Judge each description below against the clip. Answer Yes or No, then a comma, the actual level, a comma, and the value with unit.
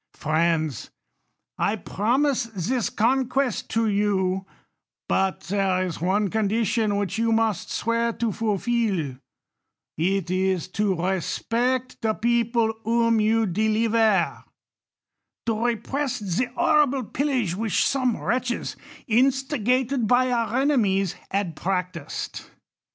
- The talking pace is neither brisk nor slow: No, slow, 105 wpm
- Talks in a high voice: Yes, high, 220 Hz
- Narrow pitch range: No, average, 3.9 semitones